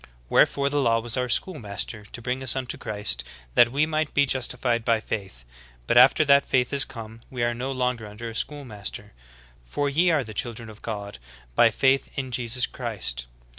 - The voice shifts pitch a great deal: No, average, 3.5 semitones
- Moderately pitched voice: No, low, 120 Hz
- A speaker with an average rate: Yes, average, 195 wpm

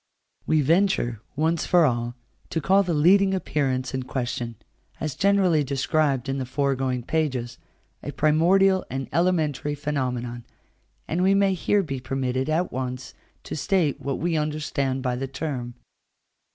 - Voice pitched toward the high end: No, medium, 145 Hz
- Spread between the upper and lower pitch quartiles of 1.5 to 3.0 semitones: No, average, 4.6 semitones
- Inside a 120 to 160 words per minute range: Yes, average, 145 wpm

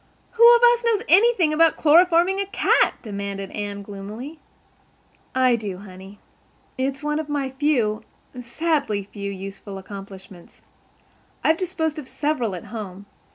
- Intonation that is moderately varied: No, wide, 8.1 semitones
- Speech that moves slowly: Yes, slow, 125 wpm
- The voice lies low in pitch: No, very high, 255 Hz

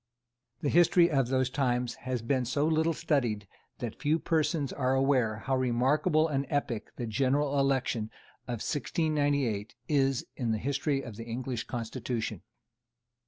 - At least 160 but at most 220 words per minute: No, average, 145 wpm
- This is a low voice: Yes, low, 130 Hz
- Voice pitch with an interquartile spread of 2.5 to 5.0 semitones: Yes, average, 3.3 semitones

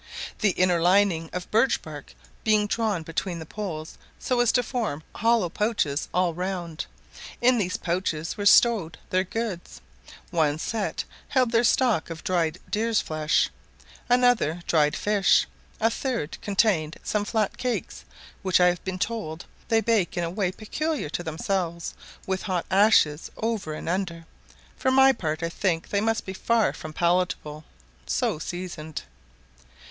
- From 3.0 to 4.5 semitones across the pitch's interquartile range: No, average, 5.2 semitones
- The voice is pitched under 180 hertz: No, medium, 185 Hz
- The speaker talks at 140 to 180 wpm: Yes, average, 150 wpm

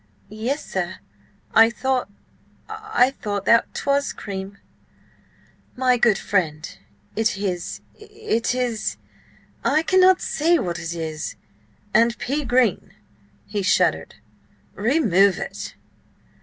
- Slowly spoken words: Yes, slow, 95 wpm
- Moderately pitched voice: No, high, 230 Hz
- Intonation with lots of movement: Yes, wide, 6.0 semitones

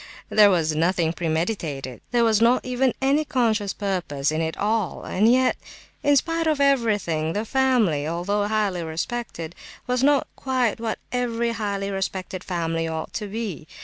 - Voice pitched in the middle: No, high, 205 Hz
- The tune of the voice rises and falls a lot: Yes, wide, 6.3 semitones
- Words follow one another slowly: No, average, 155 wpm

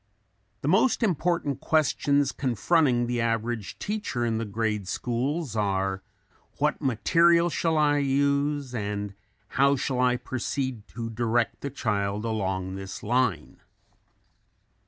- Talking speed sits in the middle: No, slow, 120 wpm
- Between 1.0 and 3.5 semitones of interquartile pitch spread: No, average, 4.7 semitones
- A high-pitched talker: No, low, 125 Hz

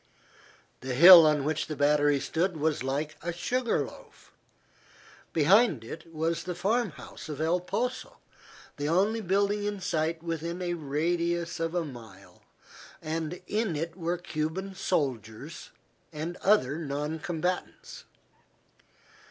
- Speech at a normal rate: No, slow, 130 wpm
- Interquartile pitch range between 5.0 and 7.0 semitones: No, average, 3.2 semitones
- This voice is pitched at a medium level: Yes, medium, 165 Hz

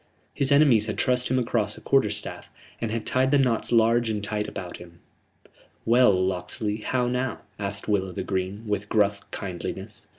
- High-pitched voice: No, low, 110 Hz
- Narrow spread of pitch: No, average, 3.6 semitones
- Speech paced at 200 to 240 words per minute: No, average, 185 wpm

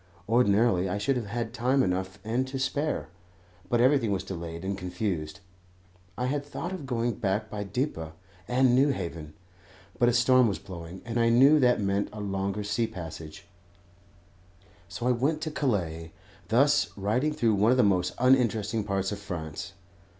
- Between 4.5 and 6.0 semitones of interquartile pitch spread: Yes, average, 4.8 semitones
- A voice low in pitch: Yes, low, 110 Hz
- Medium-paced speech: Yes, average, 165 wpm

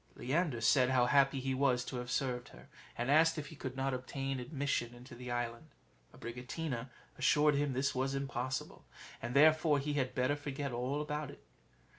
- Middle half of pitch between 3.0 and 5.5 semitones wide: No, narrow, 2.6 semitones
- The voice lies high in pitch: No, low, 135 Hz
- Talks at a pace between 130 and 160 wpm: No, average, 180 wpm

